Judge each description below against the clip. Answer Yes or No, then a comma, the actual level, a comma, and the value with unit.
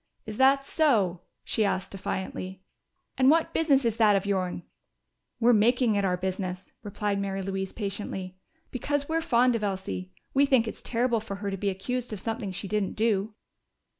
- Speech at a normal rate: Yes, average, 175 wpm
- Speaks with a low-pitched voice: No, high, 210 Hz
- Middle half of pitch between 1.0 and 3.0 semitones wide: No, average, 4.1 semitones